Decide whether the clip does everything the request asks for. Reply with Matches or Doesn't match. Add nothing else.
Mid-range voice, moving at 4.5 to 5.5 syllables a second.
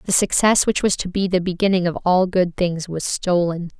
Matches